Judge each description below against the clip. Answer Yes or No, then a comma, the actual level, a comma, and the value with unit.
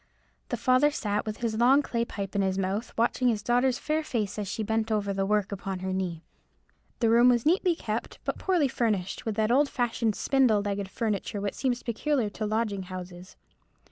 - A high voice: Yes, high, 220 Hz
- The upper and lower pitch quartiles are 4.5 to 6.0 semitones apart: No, average, 3.5 semitones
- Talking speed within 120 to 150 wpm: No, average, 200 wpm